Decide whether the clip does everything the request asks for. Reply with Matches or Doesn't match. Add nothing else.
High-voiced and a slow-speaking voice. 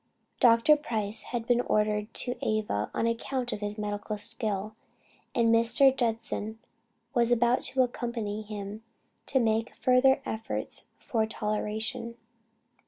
Matches